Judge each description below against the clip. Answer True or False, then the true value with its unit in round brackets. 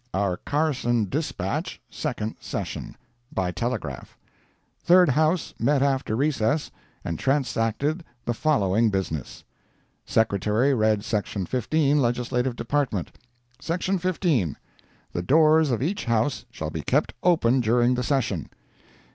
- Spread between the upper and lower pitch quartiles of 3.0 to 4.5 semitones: False (5.4 semitones)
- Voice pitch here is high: False (125 Hz)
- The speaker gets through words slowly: True (115 wpm)